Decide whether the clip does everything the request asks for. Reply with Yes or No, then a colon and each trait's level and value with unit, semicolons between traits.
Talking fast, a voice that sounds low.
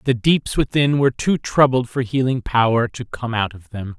Yes: fast, 210 wpm; low, 125 Hz